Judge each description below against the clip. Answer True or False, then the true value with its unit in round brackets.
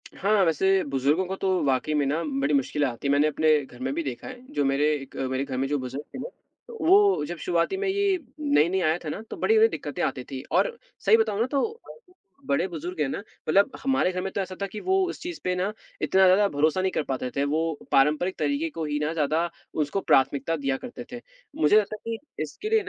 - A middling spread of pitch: False (7.4 semitones)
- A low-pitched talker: False (170 Hz)